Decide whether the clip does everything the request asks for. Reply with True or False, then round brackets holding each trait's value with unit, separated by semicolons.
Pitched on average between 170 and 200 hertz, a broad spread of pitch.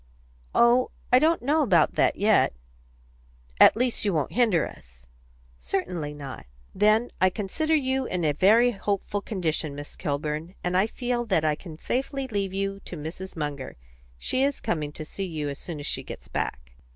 True (190 Hz; 7.6 semitones)